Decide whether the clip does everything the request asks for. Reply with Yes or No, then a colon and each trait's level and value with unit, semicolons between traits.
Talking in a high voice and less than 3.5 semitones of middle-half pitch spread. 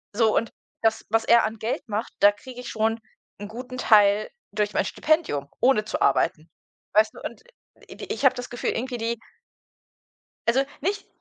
Yes: high, 225 Hz; average, 2.8 semitones